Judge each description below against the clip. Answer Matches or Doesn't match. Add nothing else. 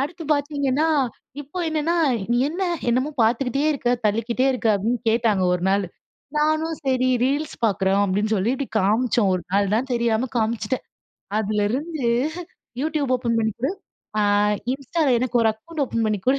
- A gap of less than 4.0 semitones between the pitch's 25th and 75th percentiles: Doesn't match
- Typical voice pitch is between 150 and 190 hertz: Doesn't match